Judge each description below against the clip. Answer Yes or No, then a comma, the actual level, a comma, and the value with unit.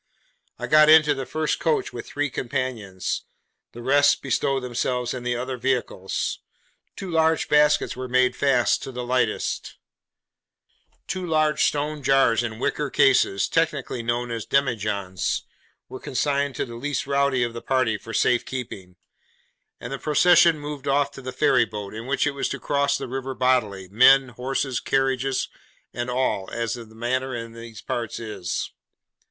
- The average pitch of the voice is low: Yes, low, 130 Hz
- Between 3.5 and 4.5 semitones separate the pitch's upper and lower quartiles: No, average, 3.1 semitones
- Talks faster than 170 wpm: No, average, 160 wpm